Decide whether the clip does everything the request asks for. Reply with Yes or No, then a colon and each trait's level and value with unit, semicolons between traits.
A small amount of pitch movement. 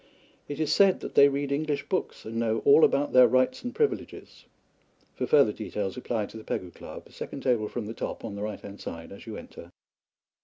No: average, 5.1 semitones